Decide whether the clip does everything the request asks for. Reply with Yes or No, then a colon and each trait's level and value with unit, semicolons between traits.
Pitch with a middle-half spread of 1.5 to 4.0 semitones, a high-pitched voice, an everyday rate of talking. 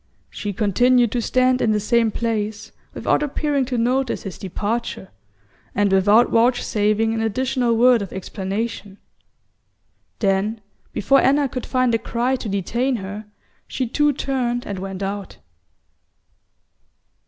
No: average, 3.6 semitones; high, 230 Hz; slow, 130 wpm